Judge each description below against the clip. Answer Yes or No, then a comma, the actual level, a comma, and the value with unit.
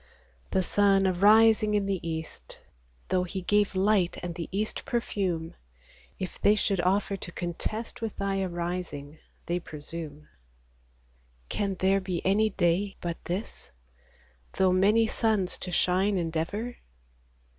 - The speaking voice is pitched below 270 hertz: Yes, high, 190 Hz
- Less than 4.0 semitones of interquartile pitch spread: Yes, average, 2.9 semitones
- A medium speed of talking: No, slow, 130 wpm